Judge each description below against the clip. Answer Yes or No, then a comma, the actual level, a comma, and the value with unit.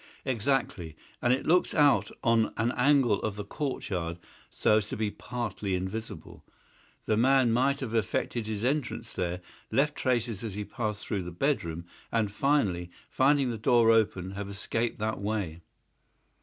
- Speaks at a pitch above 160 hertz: No, low, 110 Hz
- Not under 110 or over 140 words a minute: No, average, 155 wpm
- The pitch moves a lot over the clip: No, average, 4.2 semitones